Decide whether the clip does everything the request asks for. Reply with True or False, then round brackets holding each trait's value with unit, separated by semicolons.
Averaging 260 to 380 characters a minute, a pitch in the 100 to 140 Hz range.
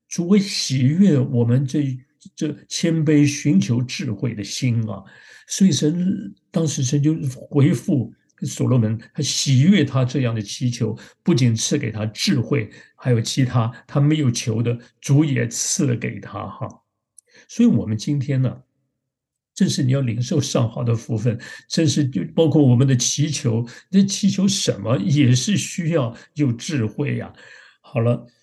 False (225 characters per minute; 135 Hz)